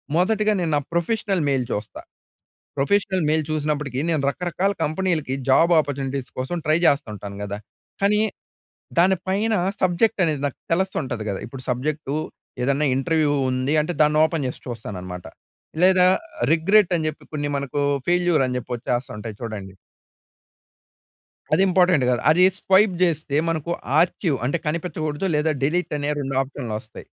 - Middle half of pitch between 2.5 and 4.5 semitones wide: No, average, 5.1 semitones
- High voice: No, medium, 155 Hz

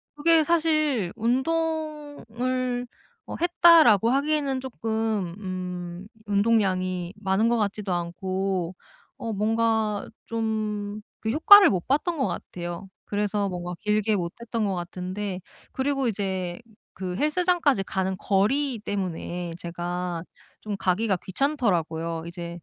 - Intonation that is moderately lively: No, wide, 5.8 semitones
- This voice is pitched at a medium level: No, high, 210 Hz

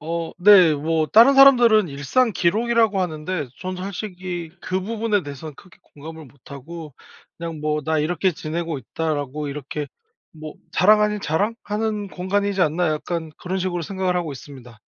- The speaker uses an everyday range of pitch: Yes, average, 4.6 semitones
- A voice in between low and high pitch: Yes, medium, 170 Hz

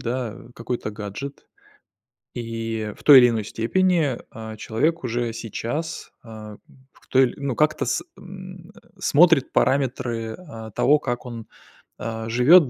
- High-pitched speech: No, low, 120 Hz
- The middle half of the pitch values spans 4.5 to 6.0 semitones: Yes, average, 5.1 semitones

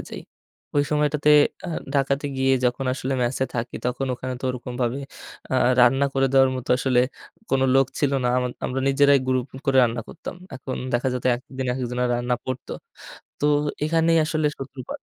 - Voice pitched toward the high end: No, low, 130 Hz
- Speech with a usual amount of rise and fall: No, narrow, 1.9 semitones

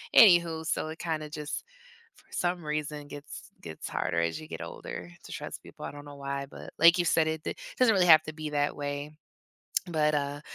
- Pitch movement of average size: No, narrow, 2.0 semitones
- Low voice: No, medium, 150 Hz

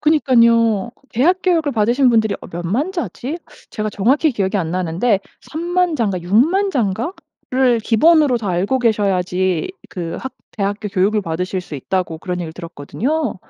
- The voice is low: No, high, 220 Hz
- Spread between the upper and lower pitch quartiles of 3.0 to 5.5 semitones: No, wide, 6.5 semitones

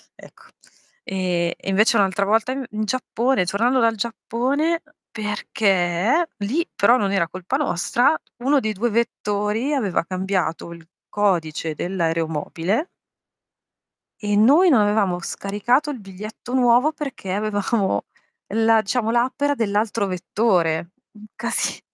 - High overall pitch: Yes, high, 210 Hz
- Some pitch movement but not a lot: Yes, average, 4.2 semitones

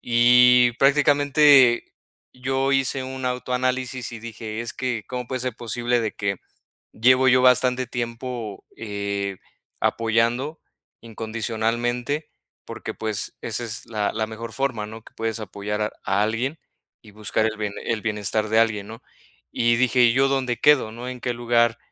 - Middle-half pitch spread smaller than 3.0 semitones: Yes, narrow, 2.6 semitones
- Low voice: Yes, low, 120 Hz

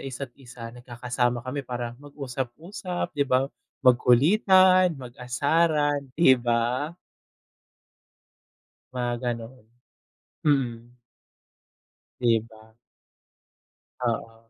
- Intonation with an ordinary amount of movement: Yes, average, 3.3 semitones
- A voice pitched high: No, low, 125 Hz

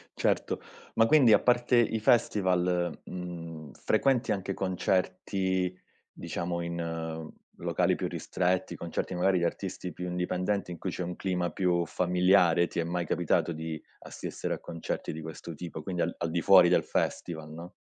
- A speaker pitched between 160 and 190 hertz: No, very low, 90 Hz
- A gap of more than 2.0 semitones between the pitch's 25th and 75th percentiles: No, narrow, 1.7 semitones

